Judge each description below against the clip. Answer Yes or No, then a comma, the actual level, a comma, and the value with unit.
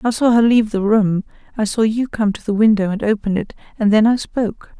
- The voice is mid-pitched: No, high, 215 Hz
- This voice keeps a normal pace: No, fast, 250 wpm